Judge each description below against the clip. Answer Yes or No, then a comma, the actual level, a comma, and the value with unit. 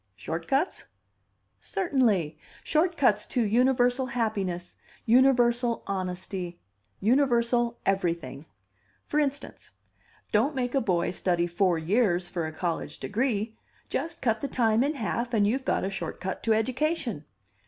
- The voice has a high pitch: Yes, high, 225 Hz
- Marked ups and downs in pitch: Yes, wide, 5.9 semitones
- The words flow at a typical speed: No, slow, 130 wpm